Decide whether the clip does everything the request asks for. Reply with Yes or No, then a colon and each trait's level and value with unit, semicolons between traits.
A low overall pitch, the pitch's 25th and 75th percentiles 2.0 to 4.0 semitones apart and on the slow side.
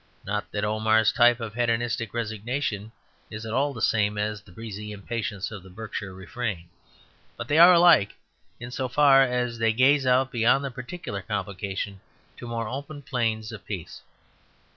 No: low, 115 Hz; average, 3.2 semitones; average, 165 wpm